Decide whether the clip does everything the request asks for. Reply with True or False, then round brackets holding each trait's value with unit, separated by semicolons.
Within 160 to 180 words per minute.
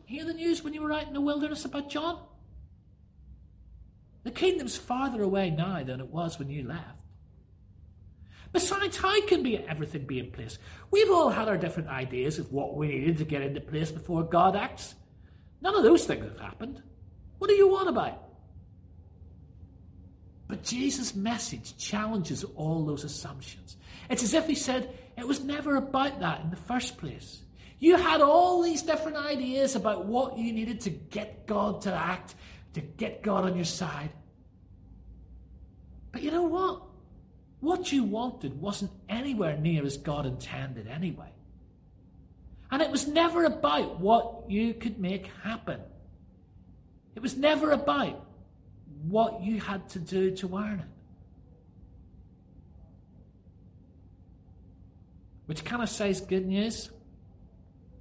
False (150 wpm)